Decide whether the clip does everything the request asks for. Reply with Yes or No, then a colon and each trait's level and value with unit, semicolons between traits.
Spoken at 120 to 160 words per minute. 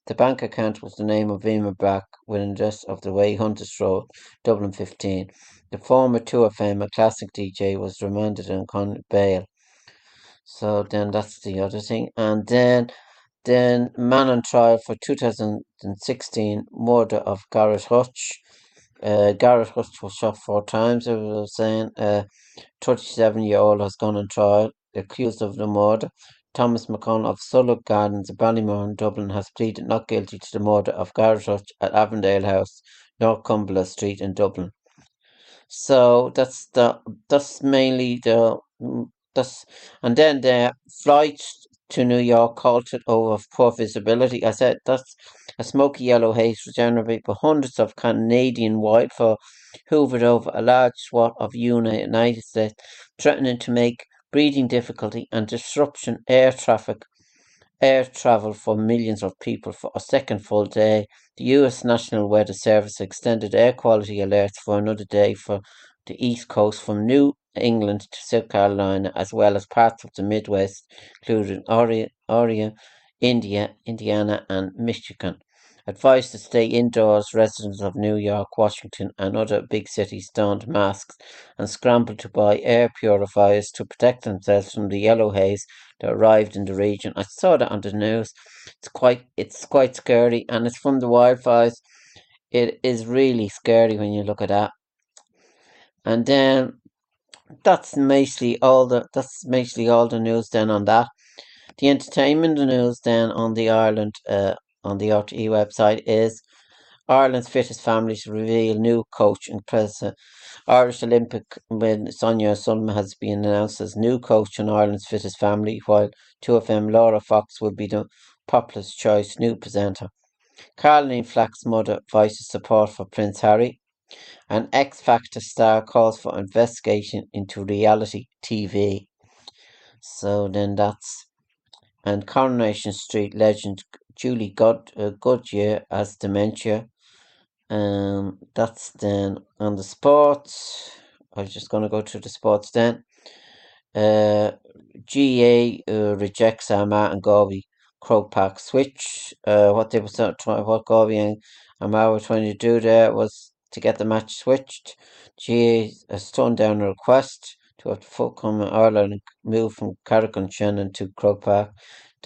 Yes: average, 150 wpm